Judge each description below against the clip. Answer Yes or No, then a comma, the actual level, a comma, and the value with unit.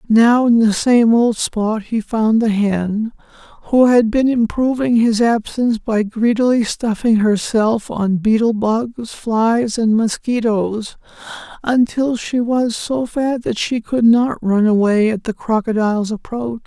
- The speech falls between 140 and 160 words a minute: Yes, average, 150 wpm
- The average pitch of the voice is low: No, high, 225 Hz